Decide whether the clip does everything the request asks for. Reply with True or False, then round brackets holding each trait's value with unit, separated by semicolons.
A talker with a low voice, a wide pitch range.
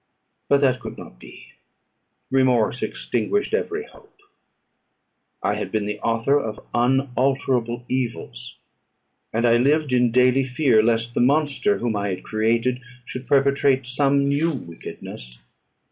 False (125 Hz; 3.2 semitones)